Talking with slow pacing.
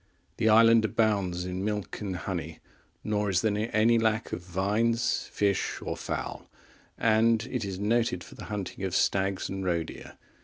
No: average, 165 wpm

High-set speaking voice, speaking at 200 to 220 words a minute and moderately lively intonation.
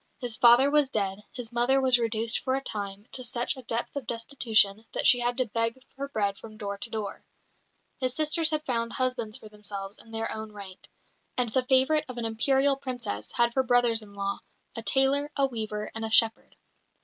Yes: high, 235 Hz; fast, 205 wpm; average, 3.3 semitones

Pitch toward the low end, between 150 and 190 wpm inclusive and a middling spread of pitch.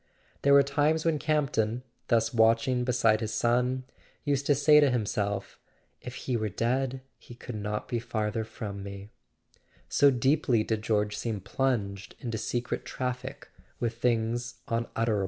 Yes: low, 120 Hz; average, 155 wpm; average, 3.1 semitones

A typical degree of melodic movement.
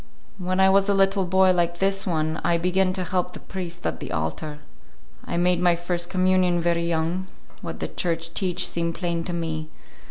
No: narrow, 1.8 semitones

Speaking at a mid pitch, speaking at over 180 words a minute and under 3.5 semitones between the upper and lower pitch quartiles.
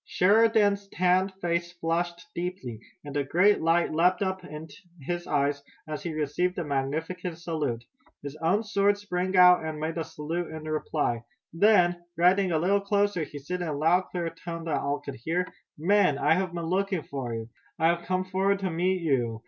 Yes: medium, 170 Hz; average, 190 wpm; average, 3.1 semitones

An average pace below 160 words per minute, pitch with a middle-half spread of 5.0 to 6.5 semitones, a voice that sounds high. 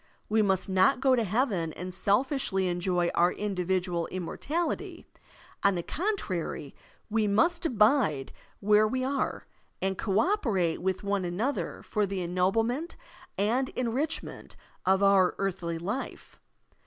Yes: slow, 135 wpm; wide, 5.4 semitones; high, 200 Hz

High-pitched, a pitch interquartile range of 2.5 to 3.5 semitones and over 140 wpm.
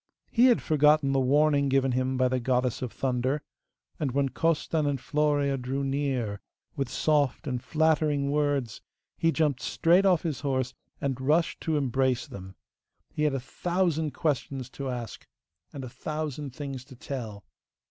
No: medium, 140 Hz; average, 2.8 semitones; average, 160 wpm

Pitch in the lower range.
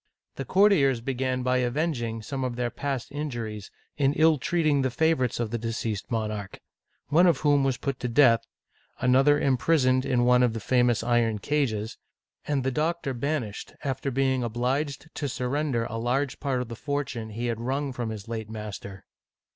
Yes: low, 125 Hz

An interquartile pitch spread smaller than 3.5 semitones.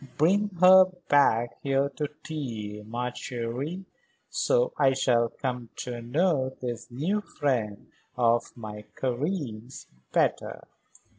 No: average, 4.3 semitones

